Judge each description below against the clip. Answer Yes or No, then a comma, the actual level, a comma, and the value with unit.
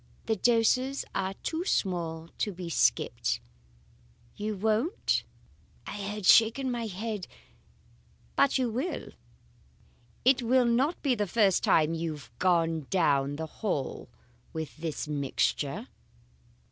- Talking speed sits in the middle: No, slow, 120 wpm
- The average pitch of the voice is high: Yes, high, 205 Hz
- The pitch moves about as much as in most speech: No, wide, 6.4 semitones